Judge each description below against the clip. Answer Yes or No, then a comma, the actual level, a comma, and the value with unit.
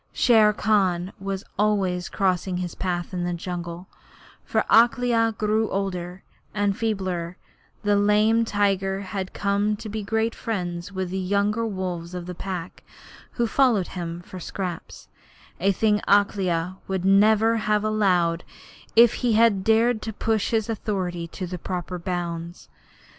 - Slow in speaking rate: No, average, 145 wpm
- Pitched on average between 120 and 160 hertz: No, high, 195 Hz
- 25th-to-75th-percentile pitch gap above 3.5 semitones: No, average, 3.2 semitones